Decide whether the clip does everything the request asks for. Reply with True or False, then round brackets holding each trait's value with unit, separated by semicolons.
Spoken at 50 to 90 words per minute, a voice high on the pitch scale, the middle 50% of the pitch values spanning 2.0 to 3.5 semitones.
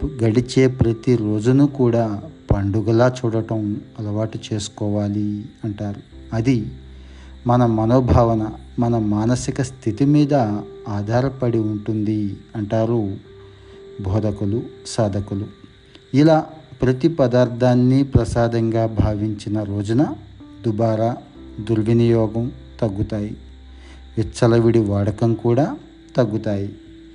False (75 wpm; 110 Hz; 3.1 semitones)